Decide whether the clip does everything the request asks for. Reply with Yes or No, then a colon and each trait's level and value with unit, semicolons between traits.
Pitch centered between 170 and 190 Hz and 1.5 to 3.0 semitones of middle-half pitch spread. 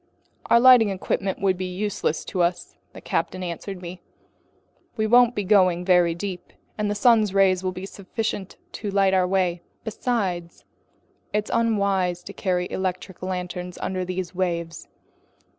Yes: medium, 185 Hz; narrow, 2.4 semitones